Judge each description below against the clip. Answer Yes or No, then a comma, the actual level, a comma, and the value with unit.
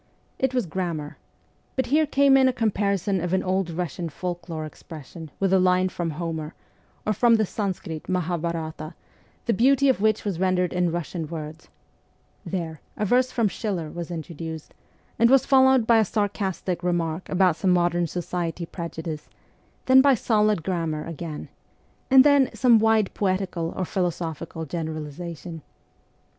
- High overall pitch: No, medium, 180 Hz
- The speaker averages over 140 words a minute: Yes, average, 155 wpm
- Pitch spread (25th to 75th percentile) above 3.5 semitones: Yes, average, 4.4 semitones